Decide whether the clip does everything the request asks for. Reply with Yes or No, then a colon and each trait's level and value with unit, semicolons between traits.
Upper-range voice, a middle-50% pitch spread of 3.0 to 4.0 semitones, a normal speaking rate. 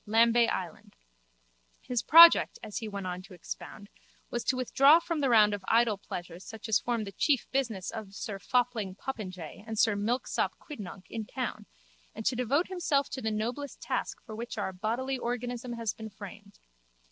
Yes: high, 225 Hz; average, 3.5 semitones; average, 180 wpm